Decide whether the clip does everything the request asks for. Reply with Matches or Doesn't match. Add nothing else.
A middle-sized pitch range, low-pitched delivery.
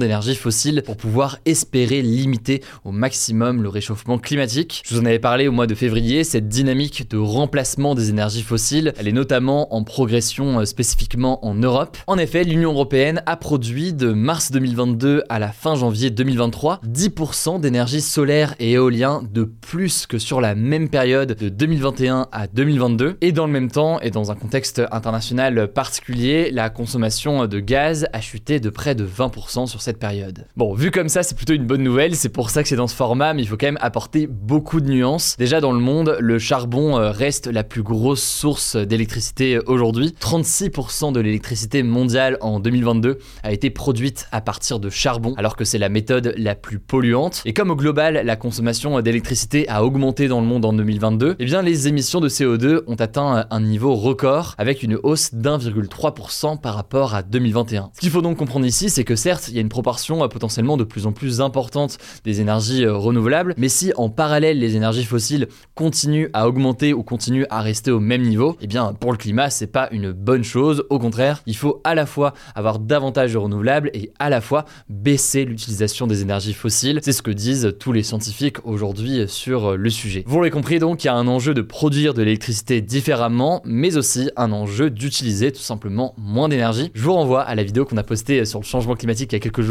Matches